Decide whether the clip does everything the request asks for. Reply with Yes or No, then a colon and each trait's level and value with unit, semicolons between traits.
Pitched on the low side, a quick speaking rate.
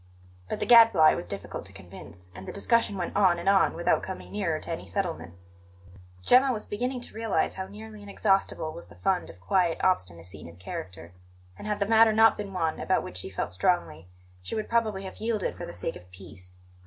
No: medium, 185 Hz; fast, 210 wpm